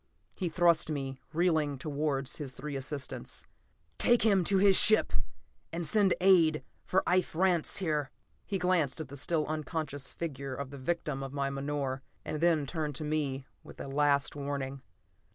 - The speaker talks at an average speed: Yes, average, 165 wpm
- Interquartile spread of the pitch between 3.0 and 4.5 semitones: Yes, average, 3.7 semitones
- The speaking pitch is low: No, medium, 150 Hz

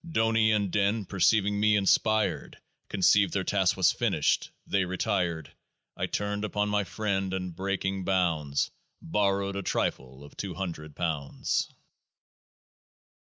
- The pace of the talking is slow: Yes, slow, 125 wpm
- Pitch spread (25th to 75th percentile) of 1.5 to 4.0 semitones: Yes, narrow, 2.6 semitones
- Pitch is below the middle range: Yes, very low, 95 Hz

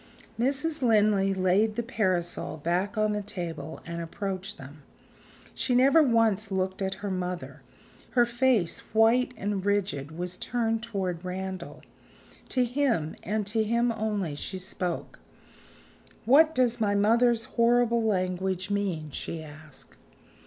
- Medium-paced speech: No, slow, 130 wpm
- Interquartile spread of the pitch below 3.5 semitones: No, average, 4.2 semitones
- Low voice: No, high, 205 Hz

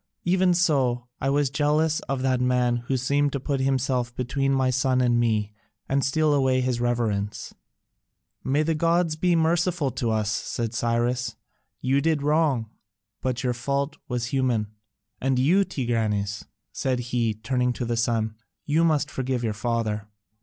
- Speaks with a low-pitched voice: Yes, low, 130 Hz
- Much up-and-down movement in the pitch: No, average, 3.3 semitones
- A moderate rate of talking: Yes, average, 160 wpm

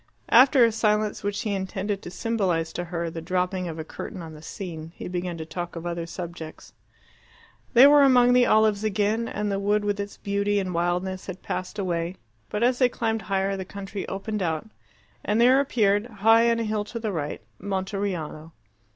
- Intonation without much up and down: No, average, 3.6 semitones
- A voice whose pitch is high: Yes, high, 200 Hz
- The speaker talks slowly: No, average, 195 wpm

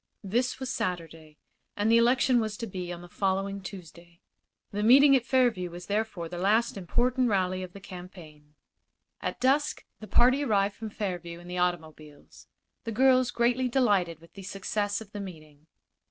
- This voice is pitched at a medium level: No, high, 195 Hz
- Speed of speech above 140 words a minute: Yes, average, 170 wpm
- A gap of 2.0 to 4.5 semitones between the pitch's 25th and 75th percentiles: No, average, 5.1 semitones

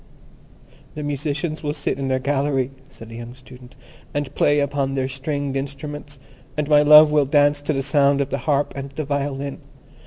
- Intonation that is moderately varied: No, narrow, 1.4 semitones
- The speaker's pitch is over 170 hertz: No, medium, 140 Hz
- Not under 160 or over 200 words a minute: Yes, average, 185 wpm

